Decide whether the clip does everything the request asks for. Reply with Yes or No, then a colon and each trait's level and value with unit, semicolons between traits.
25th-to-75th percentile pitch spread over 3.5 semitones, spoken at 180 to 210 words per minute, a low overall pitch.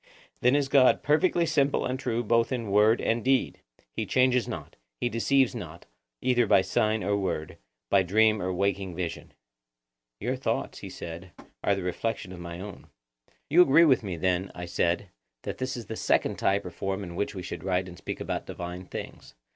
Yes: average, 5.3 semitones; average, 195 wpm; low, 100 Hz